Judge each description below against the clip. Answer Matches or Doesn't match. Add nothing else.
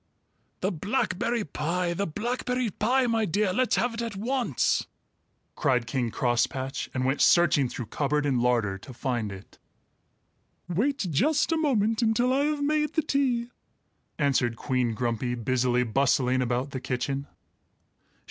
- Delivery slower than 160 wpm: Matches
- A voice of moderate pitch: Matches